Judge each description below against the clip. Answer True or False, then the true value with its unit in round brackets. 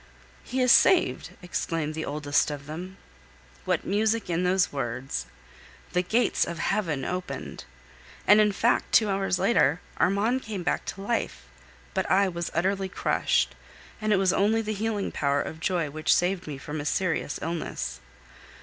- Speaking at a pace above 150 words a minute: True (160 wpm)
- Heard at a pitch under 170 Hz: False (180 Hz)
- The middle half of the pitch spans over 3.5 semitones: True (4.8 semitones)